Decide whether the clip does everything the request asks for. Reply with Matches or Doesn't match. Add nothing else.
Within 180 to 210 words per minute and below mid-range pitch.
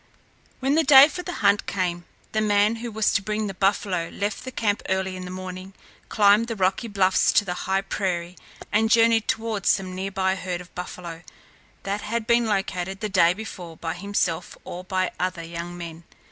Doesn't match